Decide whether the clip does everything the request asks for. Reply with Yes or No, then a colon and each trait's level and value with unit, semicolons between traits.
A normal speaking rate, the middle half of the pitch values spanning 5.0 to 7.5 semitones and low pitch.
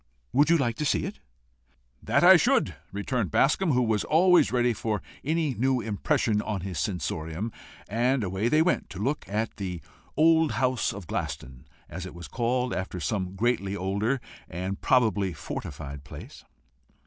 Yes: average, 160 wpm; average, 5.3 semitones; low, 110 Hz